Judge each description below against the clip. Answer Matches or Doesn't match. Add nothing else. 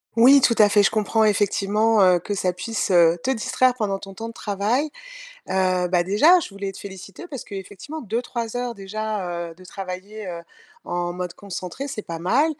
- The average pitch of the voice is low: Doesn't match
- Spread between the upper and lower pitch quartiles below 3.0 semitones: Doesn't match